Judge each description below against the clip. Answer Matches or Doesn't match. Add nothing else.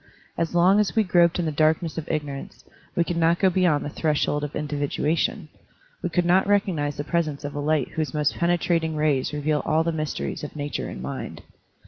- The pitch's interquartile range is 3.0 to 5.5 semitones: Doesn't match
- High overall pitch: Doesn't match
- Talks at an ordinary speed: Doesn't match